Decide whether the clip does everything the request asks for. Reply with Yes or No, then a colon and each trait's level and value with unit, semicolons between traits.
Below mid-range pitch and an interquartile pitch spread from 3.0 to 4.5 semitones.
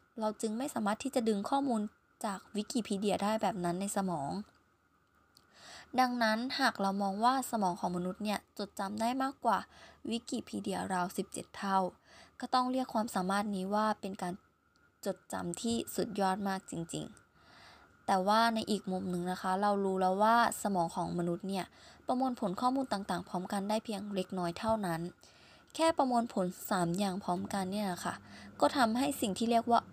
No: high, 200 Hz; average, 3.8 semitones